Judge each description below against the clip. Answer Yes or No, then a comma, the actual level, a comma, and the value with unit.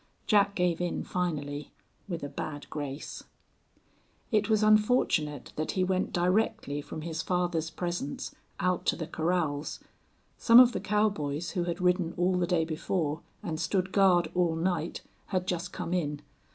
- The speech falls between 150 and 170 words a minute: Yes, average, 155 wpm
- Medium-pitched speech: Yes, medium, 175 Hz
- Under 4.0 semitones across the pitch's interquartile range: Yes, average, 2.8 semitones